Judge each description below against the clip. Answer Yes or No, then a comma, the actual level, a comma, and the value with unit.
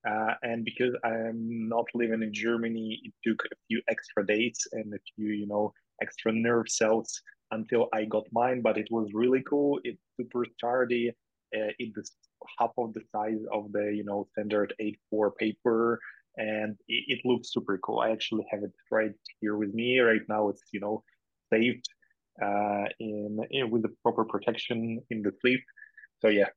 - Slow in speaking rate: No, average, 180 wpm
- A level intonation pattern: Yes, narrow, 1.8 semitones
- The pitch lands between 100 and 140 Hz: Yes, low, 110 Hz